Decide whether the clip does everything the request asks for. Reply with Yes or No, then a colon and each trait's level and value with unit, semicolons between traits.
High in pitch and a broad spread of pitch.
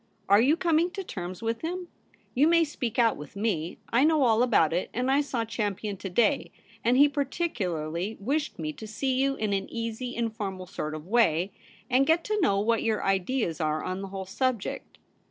Yes: high, 225 Hz; wide, 6.0 semitones